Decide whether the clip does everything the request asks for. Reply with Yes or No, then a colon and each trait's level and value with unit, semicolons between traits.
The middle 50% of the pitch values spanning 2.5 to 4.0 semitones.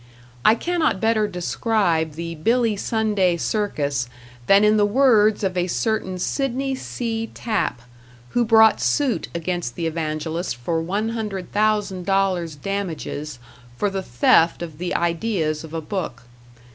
No: average, 4.9 semitones